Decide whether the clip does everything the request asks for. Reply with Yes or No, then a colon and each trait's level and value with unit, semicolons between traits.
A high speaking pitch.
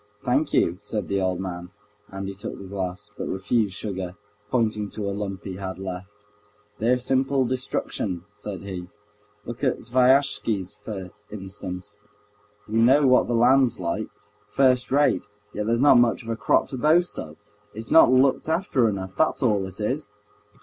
No: low, 105 Hz